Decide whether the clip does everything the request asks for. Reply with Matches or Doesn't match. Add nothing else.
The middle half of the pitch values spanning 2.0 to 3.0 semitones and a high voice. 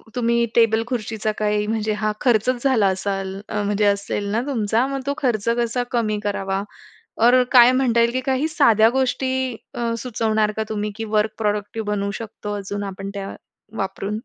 Matches